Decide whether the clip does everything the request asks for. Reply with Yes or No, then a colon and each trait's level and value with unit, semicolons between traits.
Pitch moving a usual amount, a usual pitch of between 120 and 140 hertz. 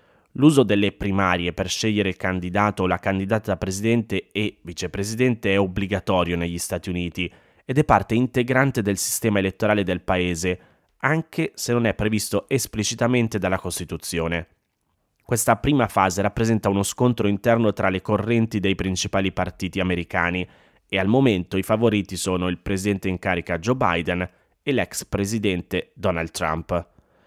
No: average, 3.4 semitones; low, 100 Hz